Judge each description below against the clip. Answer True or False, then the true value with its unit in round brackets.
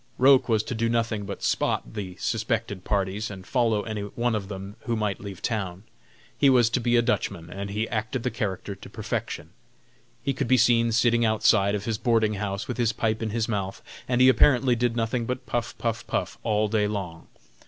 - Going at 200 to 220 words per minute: True (205 wpm)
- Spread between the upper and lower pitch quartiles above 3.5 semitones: False (2.6 semitones)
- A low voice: True (110 Hz)